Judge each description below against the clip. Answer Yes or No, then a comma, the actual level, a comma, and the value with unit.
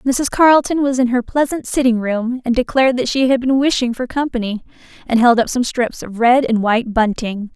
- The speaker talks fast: Yes, fast, 215 wpm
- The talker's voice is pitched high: Yes, high, 245 Hz